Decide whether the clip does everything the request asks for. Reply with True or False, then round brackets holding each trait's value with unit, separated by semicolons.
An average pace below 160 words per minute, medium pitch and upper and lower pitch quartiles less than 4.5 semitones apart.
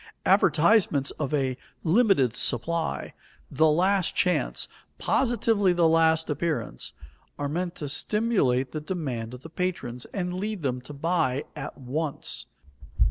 False (135 wpm; 160 Hz; 4.8 semitones)